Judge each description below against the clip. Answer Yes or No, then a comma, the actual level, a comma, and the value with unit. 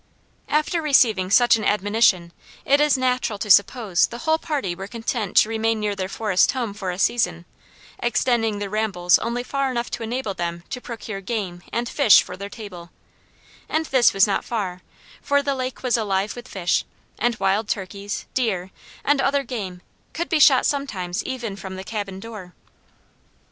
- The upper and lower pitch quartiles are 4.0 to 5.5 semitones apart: Yes, average, 4.6 semitones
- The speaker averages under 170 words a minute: No, average, 175 wpm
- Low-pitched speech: No, high, 220 Hz